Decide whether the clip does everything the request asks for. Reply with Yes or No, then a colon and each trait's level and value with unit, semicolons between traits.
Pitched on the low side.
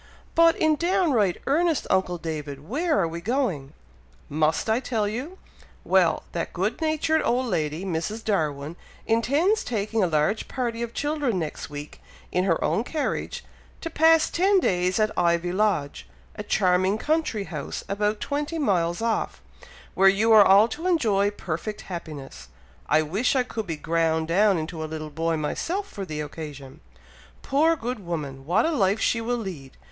No: high, 200 Hz